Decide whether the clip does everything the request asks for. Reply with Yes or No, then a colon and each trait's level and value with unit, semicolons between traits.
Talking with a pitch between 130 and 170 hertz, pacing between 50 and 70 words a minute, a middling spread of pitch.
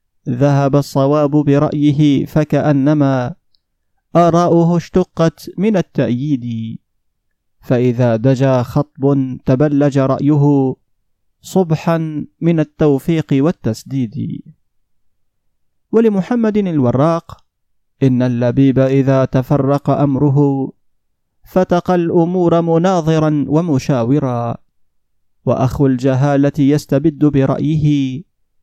Yes: medium, 140 Hz; slow, 65 wpm; average, 3.2 semitones